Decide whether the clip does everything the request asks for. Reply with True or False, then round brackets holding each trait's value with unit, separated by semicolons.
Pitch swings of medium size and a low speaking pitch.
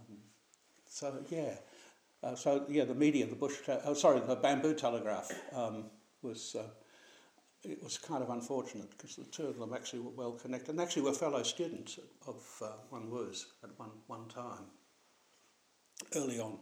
True (3.9 semitones; 125 Hz)